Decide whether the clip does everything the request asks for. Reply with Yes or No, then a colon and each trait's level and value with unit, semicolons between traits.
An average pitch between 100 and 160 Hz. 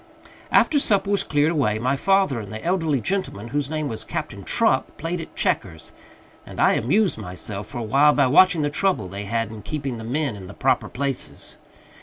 Yes: medium, 140 Hz